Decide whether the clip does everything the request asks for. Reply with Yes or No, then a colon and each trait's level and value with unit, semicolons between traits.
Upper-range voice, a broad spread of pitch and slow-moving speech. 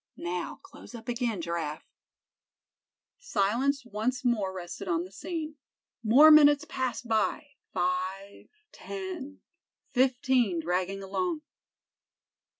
Yes: high, 230 Hz; wide, 6.9 semitones; slow, 95 wpm